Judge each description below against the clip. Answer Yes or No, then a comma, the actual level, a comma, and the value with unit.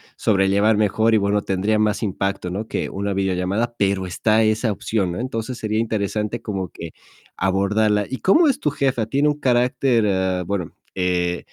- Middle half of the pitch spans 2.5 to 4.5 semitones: Yes, average, 2.8 semitones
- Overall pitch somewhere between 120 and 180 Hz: No, low, 105 Hz